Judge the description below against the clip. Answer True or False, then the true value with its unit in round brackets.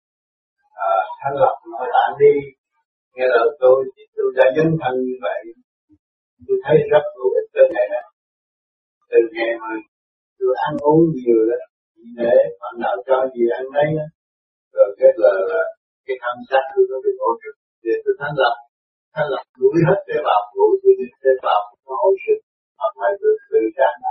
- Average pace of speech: False (140 wpm)